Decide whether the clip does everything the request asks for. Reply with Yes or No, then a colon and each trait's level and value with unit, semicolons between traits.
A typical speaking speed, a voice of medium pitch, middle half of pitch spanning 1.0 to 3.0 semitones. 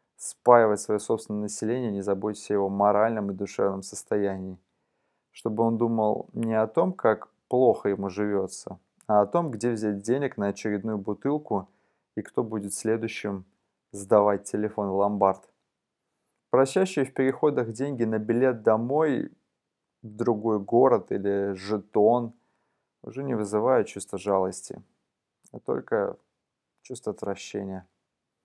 No: average, 125 wpm; low, 105 Hz; average, 2.7 semitones